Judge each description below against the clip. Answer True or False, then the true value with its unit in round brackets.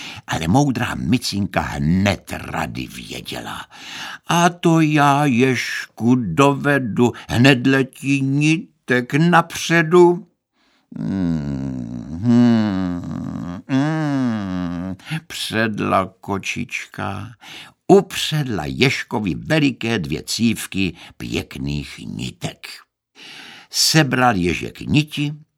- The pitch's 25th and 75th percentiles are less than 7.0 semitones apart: False (8.7 semitones)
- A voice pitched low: True (125 Hz)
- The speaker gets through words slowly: True (65 wpm)